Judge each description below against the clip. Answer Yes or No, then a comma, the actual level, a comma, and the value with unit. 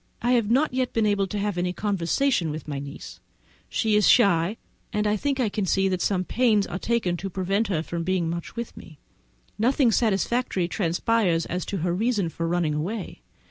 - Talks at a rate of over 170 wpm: Yes, average, 190 wpm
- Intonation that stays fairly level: No, average, 4.4 semitones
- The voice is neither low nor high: No, high, 195 Hz